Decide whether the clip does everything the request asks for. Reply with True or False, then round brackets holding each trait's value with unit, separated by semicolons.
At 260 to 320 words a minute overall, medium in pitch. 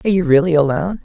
False (230 wpm; 170 Hz)